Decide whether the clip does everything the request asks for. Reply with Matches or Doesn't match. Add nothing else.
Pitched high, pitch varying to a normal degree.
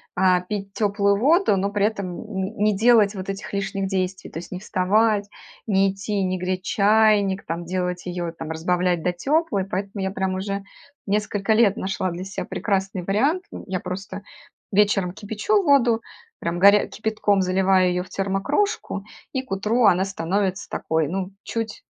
Doesn't match